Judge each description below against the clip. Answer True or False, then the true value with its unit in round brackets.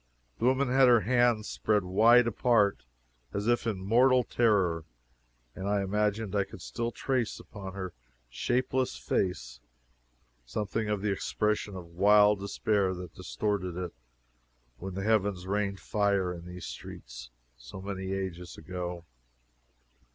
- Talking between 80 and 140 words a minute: True (135 wpm)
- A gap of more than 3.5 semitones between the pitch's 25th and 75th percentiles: False (3.2 semitones)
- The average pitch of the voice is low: True (100 Hz)